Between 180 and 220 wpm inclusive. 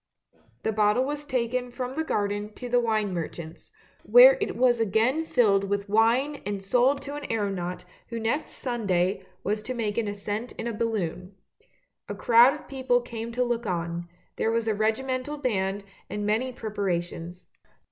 No: average, 165 wpm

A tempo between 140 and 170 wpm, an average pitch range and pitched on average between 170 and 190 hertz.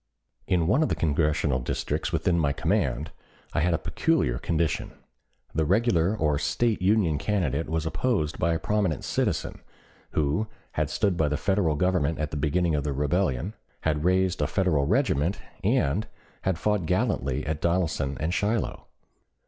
No: average, 160 wpm; average, 4.2 semitones; very low, 80 Hz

